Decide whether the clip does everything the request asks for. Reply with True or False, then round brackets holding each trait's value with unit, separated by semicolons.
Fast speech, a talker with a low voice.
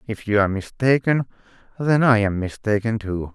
False (145 wpm; 110 Hz)